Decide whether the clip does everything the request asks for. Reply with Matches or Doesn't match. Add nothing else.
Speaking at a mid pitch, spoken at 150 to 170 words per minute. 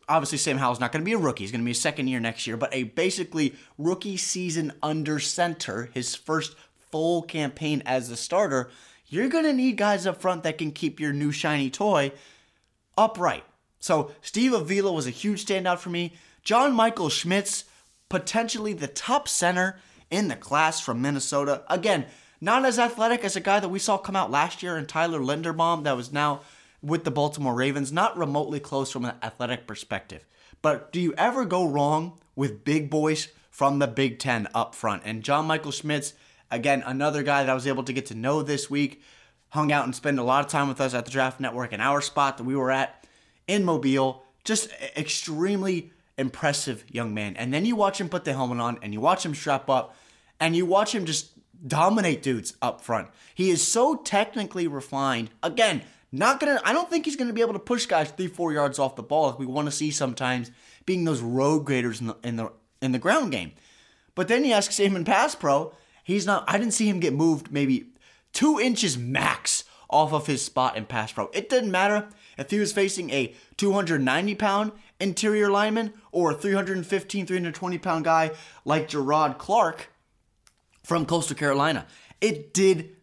Doesn't match